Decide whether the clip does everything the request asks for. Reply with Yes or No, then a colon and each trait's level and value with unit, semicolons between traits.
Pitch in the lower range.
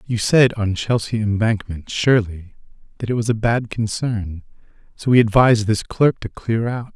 Yes: low, 110 Hz